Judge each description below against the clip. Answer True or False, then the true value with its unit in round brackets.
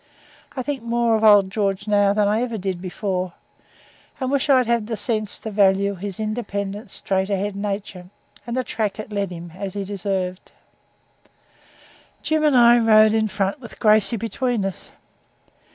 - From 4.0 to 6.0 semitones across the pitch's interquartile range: False (2.9 semitones)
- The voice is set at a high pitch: True (210 Hz)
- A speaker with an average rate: True (170 wpm)